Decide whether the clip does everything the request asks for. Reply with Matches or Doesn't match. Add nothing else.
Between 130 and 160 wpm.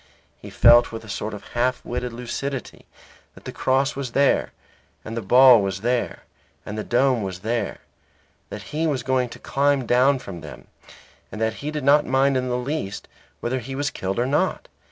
Doesn't match